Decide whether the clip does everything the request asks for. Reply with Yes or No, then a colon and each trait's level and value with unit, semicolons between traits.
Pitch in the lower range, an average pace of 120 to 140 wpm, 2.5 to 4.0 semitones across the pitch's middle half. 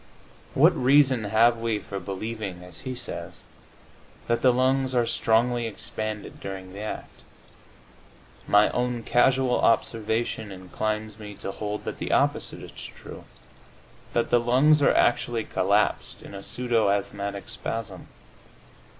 Yes: low, 110 Hz; slow, 135 wpm; average, 3.0 semitones